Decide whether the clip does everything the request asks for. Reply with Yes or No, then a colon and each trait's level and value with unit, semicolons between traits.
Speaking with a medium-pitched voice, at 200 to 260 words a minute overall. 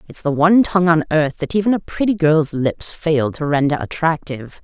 Yes: medium, 160 Hz; fast, 205 wpm